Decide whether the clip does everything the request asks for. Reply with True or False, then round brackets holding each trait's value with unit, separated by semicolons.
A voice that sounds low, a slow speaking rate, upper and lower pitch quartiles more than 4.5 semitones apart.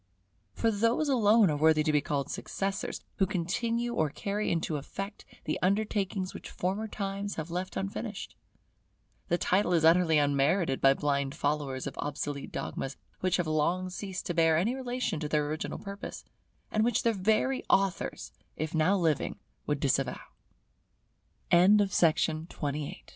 False (185 Hz; 130 wpm; 5.2 semitones)